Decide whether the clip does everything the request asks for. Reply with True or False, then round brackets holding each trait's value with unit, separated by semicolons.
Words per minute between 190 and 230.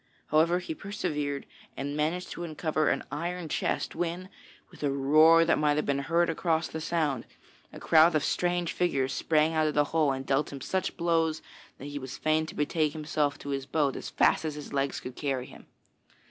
True (200 wpm)